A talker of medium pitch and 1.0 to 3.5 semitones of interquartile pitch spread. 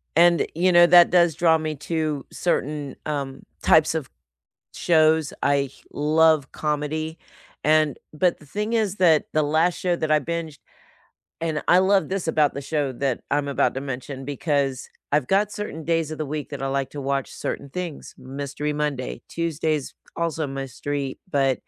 Yes: medium, 155 Hz; average, 2.9 semitones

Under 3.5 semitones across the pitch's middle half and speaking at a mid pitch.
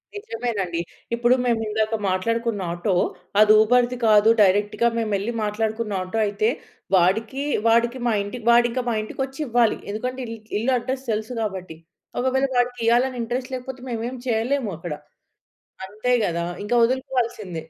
No: average, 3.0 semitones; high, 230 Hz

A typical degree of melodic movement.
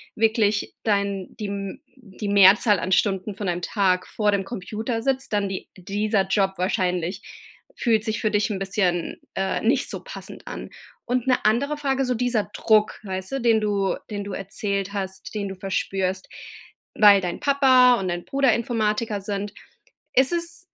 Yes: average, 3.2 semitones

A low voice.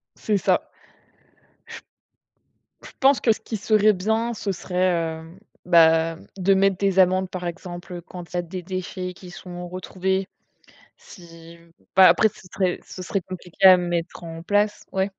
No: medium, 185 Hz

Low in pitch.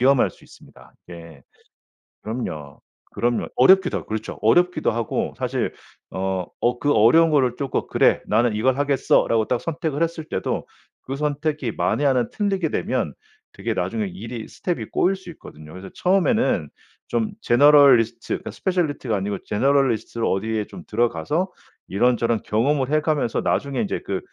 Yes: low, 125 Hz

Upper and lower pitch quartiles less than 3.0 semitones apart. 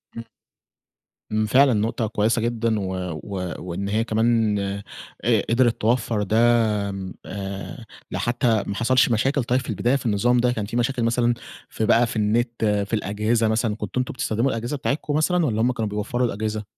Yes: narrow, 2.4 semitones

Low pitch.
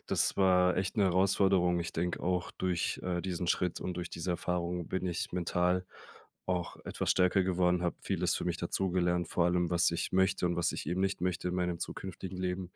Yes: very low, 90 Hz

